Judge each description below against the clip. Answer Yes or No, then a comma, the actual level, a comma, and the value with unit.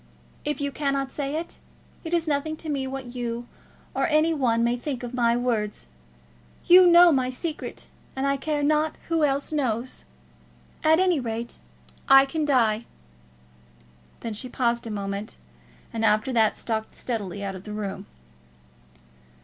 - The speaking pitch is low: No, very high, 260 Hz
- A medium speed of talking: Yes, average, 160 wpm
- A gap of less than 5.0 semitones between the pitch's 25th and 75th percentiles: Yes, average, 4.5 semitones